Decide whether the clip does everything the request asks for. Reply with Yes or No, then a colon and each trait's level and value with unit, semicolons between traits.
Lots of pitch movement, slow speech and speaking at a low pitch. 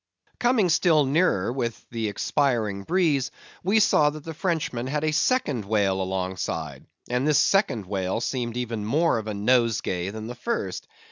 No: wide, 6.6 semitones; average, 160 wpm; low, 125 Hz